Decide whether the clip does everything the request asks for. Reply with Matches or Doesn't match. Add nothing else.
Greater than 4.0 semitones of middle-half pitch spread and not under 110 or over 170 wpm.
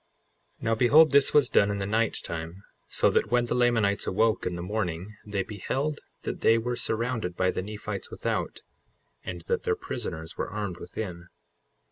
Doesn't match